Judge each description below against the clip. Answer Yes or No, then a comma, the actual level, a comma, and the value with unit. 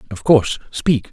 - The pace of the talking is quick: No, average, 160 wpm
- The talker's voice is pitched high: No, low, 125 Hz